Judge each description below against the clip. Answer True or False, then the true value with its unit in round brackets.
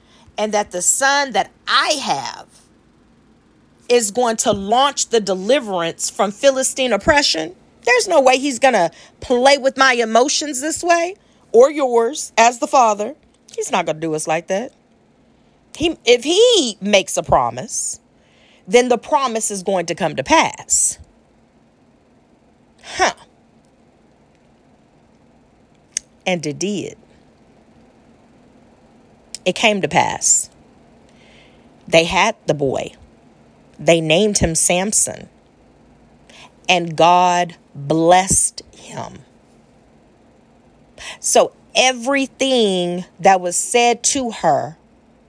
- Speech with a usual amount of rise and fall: False (6.6 semitones)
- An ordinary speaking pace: False (110 wpm)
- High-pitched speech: True (230 Hz)